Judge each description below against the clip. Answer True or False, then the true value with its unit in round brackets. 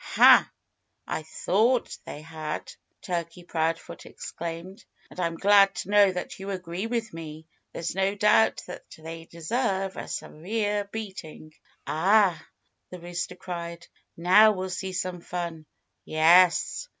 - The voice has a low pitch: False (180 Hz)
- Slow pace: True (130 wpm)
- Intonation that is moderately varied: True (3.2 semitones)